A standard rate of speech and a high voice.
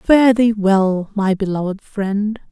Yes: average, 145 wpm; high, 205 Hz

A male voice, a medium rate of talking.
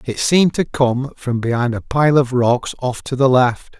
No: male; fast, 220 wpm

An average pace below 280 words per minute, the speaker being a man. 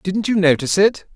Yes: fast, 210 wpm; male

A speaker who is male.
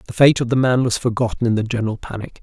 Yes: male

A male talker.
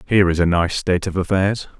Yes: male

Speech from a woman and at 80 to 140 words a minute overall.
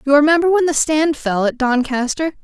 No: female; average, 200 wpm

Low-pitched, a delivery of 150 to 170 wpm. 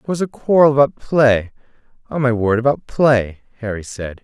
Yes: low, 125 Hz; average, 155 wpm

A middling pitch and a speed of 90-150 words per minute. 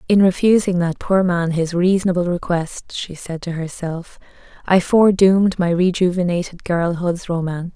Yes: medium, 175 Hz; average, 140 wpm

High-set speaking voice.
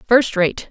Yes: high, 215 Hz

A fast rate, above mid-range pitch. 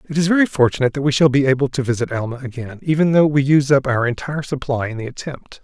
No: fast, 255 wpm; low, 135 Hz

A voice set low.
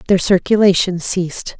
No: medium, 185 Hz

